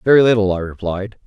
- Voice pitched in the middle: No, low, 105 Hz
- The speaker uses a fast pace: No, average, 190 wpm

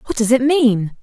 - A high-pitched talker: Yes, high, 240 Hz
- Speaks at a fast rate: Yes, fast, 235 wpm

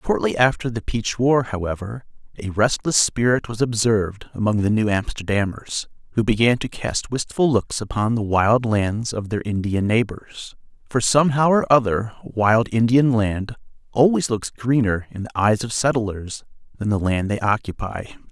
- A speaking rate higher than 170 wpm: No, average, 160 wpm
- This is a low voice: Yes, low, 115 Hz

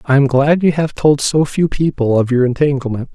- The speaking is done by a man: Yes, male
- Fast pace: Yes, fast, 230 wpm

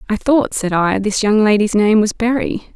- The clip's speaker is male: No, female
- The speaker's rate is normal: No, fast, 220 wpm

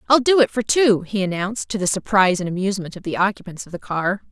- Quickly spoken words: Yes, fast, 250 wpm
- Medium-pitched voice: No, high, 200 Hz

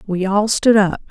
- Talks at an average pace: No, fast, 220 wpm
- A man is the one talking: No, female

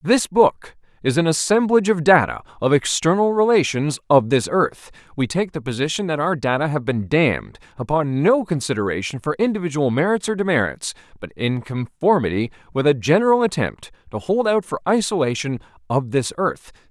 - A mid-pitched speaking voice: Yes, medium, 155 Hz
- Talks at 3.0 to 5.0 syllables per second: No, 5.4 syllables/s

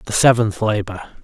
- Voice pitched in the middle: No, low, 110 Hz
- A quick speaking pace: No, average, 145 wpm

